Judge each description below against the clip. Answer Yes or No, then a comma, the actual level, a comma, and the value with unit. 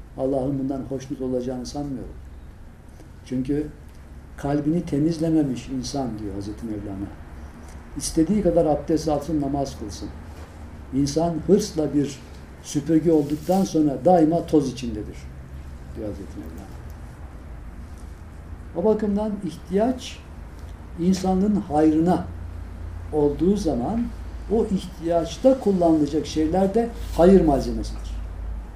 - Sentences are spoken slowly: Yes, slow, 90 wpm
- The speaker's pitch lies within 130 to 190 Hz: Yes, low, 135 Hz